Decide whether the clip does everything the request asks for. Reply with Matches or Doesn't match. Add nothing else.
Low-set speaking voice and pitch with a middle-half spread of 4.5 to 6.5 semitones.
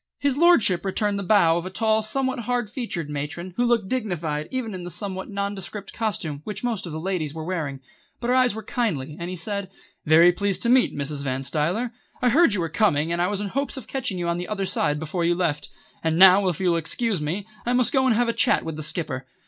Doesn't match